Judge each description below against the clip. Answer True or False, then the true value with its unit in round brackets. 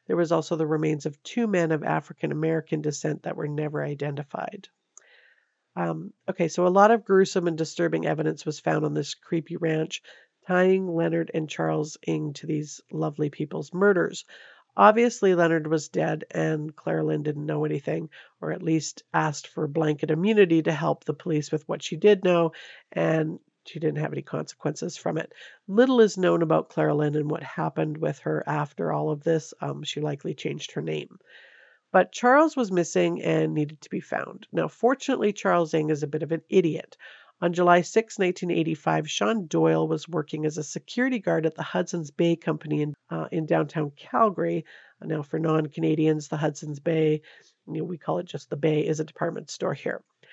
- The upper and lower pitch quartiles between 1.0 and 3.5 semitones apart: True (2.6 semitones)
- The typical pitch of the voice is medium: True (160 Hz)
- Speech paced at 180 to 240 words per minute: True (185 wpm)